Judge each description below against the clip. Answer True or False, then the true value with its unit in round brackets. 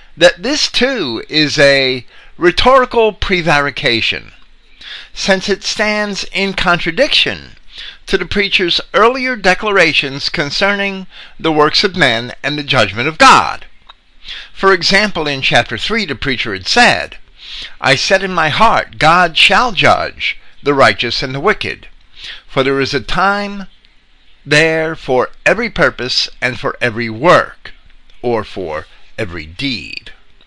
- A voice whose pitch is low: False (160 Hz)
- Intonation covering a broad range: True (6.6 semitones)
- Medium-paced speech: False (130 wpm)